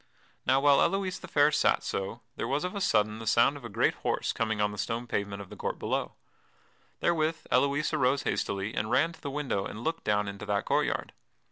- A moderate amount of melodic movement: No, wide, 6.1 semitones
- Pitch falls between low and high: No, low, 120 Hz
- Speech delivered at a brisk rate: Yes, fast, 225 wpm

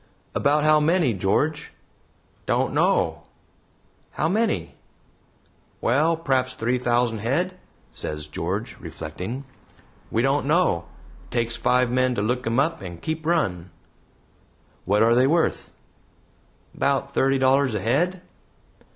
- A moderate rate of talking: No, slow, 120 wpm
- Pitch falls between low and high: No, low, 130 Hz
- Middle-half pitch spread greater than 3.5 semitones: Yes, average, 5.1 semitones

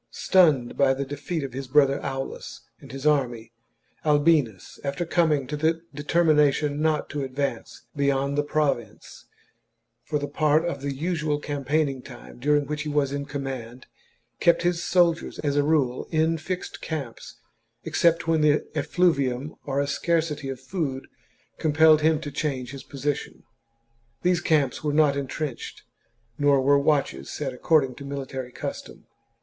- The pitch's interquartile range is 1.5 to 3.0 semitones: Yes, narrow, 2.5 semitones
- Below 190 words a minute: Yes, average, 155 wpm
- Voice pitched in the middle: Yes, medium, 145 Hz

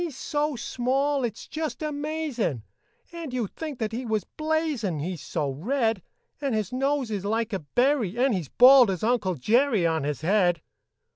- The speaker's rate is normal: Yes, average, 185 wpm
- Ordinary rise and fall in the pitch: No, wide, 6.7 semitones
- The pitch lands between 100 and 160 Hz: No, high, 240 Hz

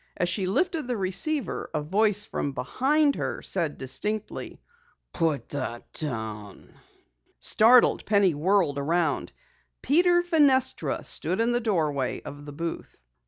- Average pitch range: No, wide, 9.0 semitones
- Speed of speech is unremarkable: No, slow, 125 wpm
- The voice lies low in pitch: No, medium, 185 Hz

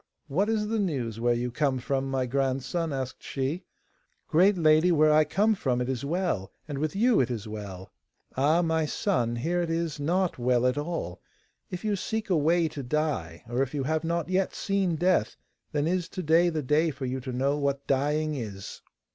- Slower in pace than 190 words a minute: No, fast, 205 wpm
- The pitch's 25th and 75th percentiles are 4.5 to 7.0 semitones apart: Yes, average, 4.9 semitones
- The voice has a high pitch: No, medium, 150 Hz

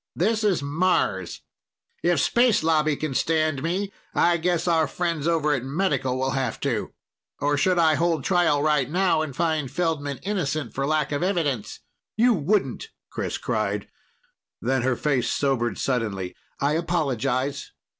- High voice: No, medium, 155 Hz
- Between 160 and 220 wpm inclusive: No, average, 150 wpm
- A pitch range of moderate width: Yes, average, 4.2 semitones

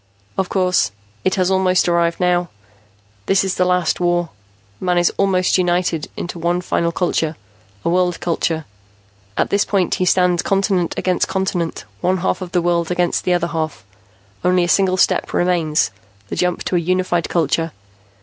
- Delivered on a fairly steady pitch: Yes, narrow, 1.3 semitones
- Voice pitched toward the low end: No, medium, 180 Hz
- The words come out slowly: No, average, 170 wpm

